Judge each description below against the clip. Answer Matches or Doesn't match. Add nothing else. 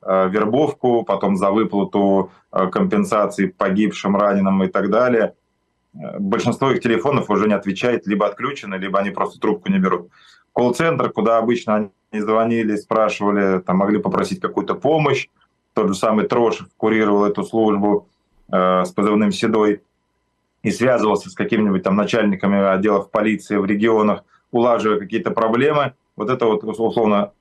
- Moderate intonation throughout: Doesn't match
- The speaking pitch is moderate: Doesn't match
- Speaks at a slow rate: Doesn't match